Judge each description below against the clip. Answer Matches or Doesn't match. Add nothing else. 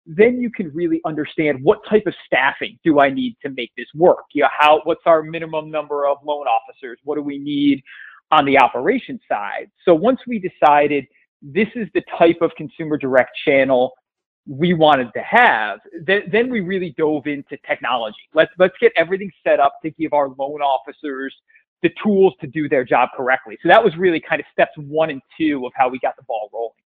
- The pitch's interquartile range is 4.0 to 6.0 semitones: Matches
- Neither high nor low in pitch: Matches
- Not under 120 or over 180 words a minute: Doesn't match